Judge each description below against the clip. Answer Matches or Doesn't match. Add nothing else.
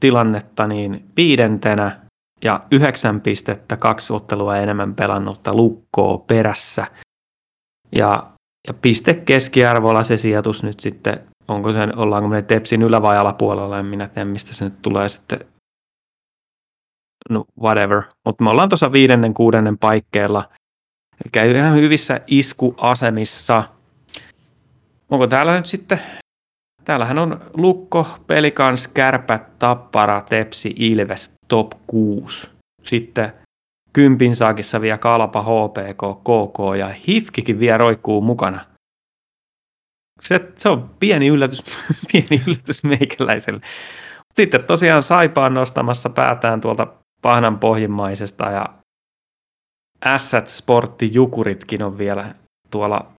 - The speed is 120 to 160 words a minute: Doesn't match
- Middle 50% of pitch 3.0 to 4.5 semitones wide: Matches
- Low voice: Matches